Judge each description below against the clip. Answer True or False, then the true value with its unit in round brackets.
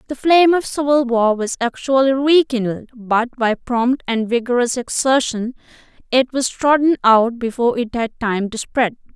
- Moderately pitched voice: False (245 Hz)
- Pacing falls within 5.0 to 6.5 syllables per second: False (4.7 syllables/s)